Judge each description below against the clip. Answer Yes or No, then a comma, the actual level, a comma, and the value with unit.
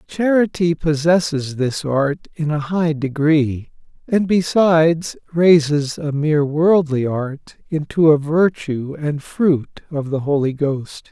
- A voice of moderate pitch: Yes, medium, 155 Hz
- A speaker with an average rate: No, slow, 130 wpm